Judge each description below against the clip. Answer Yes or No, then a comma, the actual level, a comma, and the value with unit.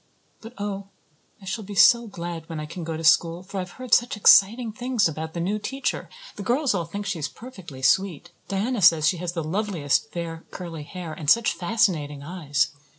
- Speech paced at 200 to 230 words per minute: Yes, fast, 205 wpm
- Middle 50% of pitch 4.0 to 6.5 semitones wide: Yes, average, 4.3 semitones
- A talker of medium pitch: Yes, medium, 180 Hz